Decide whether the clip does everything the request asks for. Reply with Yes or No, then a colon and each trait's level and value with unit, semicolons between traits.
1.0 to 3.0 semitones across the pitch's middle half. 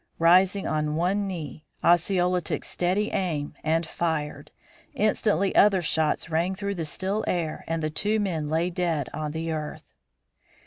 No: average, 3.4 semitones